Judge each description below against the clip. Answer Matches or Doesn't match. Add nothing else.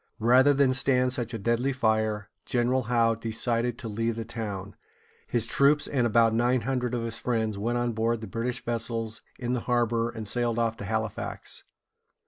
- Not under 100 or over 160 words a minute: Doesn't match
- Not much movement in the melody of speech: Matches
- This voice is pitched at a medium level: Doesn't match